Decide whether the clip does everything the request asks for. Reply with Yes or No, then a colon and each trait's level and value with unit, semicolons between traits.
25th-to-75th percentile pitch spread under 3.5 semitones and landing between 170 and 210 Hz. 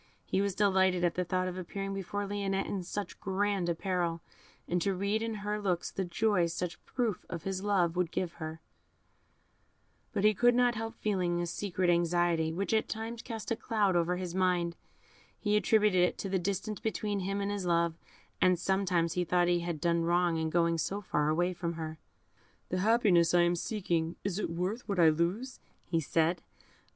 Yes: average, 2.9 semitones; medium, 185 Hz